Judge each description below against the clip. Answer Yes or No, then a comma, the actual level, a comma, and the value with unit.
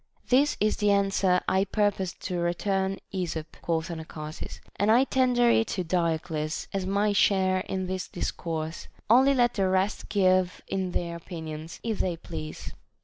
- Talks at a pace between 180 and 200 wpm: No, average, 165 wpm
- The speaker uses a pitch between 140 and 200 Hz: Yes, medium, 185 Hz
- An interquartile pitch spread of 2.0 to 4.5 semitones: Yes, average, 3.3 semitones